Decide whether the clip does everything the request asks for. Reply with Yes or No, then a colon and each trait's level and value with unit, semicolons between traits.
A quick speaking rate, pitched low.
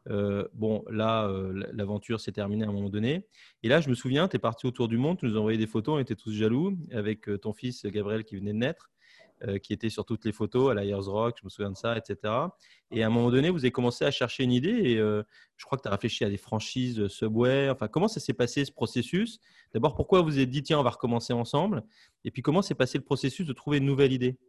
Yes: fast, 270 wpm; low, 120 Hz